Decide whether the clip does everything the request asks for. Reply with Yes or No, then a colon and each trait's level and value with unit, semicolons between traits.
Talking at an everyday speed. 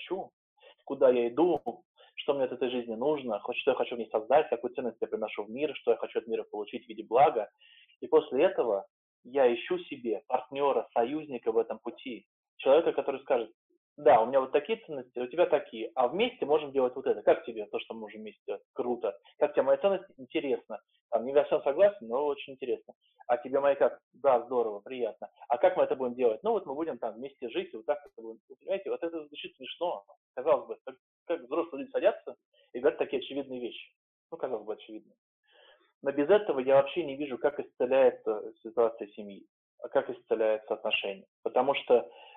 No: fast, 200 wpm